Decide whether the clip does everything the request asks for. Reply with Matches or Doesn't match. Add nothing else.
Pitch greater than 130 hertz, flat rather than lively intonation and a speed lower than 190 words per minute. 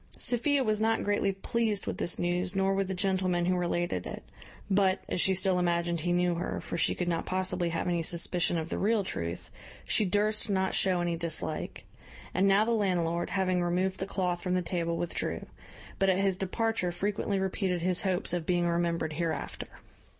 Doesn't match